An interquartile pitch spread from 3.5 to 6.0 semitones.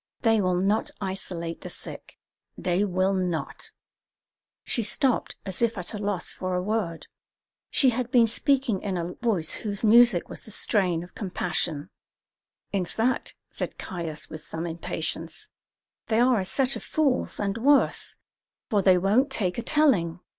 Yes: average, 4.6 semitones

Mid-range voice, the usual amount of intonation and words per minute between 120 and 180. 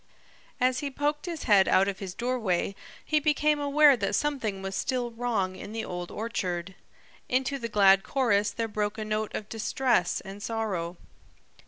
No: high, 220 Hz; average, 4.9 semitones; average, 170 wpm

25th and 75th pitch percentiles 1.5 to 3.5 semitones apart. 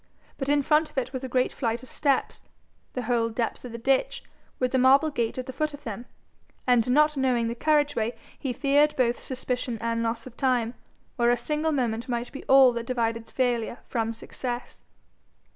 Yes: narrow, 2.6 semitones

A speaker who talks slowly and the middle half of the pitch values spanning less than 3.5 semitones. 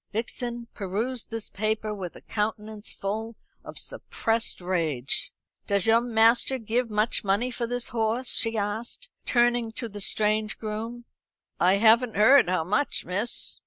No: average, 145 wpm; narrow, 2.5 semitones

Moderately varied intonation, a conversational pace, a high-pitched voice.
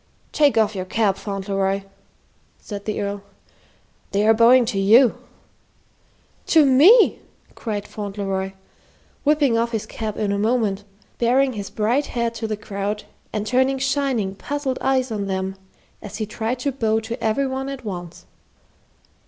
Yes: average, 4.2 semitones; average, 150 wpm; high, 220 Hz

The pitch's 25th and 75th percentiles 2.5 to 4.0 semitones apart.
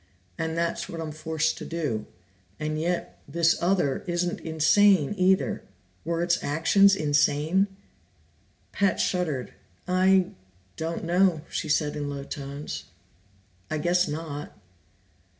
Yes: average, 3.0 semitones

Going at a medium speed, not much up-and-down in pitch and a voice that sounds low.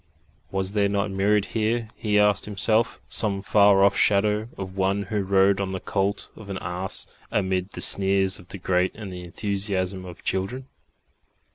Yes: average, 170 wpm; narrow, 1.6 semitones; low, 100 Hz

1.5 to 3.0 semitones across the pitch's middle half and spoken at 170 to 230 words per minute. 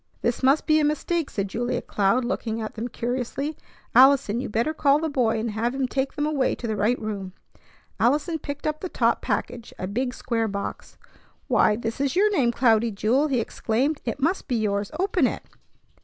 No: average, 4.4 semitones; average, 200 wpm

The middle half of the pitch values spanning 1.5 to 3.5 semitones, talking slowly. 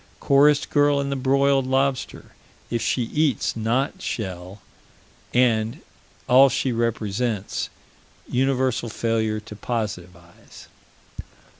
No: average, 3.9 semitones; slow, 100 wpm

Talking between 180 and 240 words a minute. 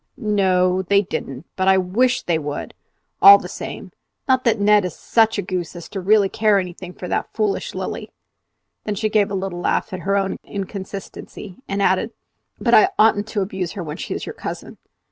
Yes: average, 200 wpm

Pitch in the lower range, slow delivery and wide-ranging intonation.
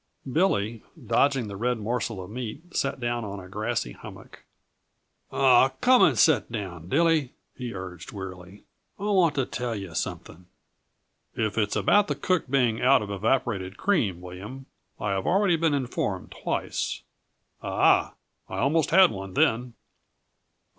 No: low, 115 Hz; average, 150 wpm; wide, 6.1 semitones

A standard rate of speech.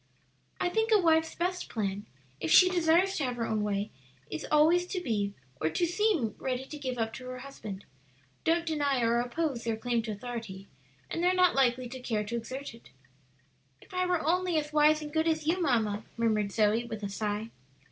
No: fast, 210 wpm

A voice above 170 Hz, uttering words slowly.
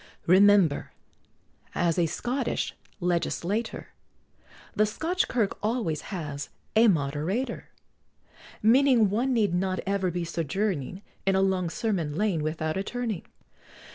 Yes: high, 190 Hz; slow, 115 wpm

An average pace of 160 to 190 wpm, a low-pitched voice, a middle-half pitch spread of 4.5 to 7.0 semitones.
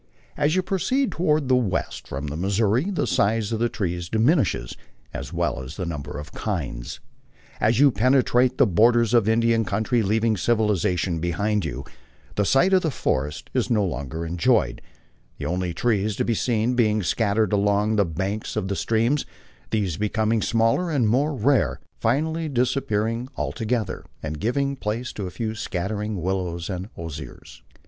Yes: average, 165 wpm; low, 110 Hz; average, 4.8 semitones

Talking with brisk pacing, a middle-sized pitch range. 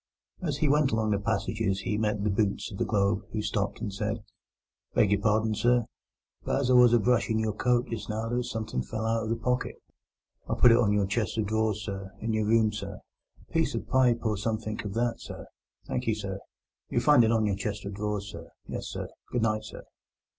No: fast, 225 wpm; narrow, 2.0 semitones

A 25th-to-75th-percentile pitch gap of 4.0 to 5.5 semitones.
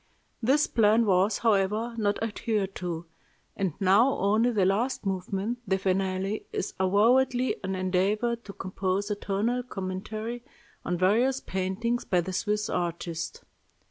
No: average, 3.6 semitones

